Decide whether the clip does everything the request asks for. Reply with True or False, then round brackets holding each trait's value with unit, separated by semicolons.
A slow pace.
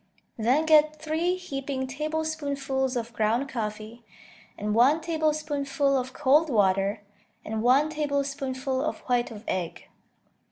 True (120 wpm)